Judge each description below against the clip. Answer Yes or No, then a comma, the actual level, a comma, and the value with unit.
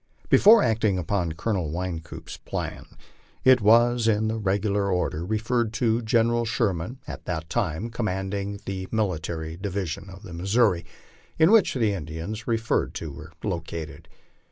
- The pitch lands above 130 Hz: No, low, 100 Hz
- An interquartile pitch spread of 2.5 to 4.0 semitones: No, average, 4.8 semitones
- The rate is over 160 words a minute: No, average, 145 wpm